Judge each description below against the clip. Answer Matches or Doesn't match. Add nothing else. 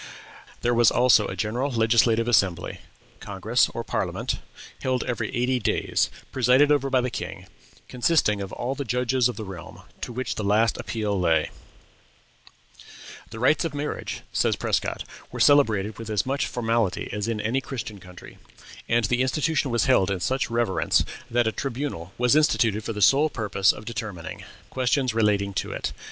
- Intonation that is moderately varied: Matches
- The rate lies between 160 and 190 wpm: Matches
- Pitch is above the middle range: Doesn't match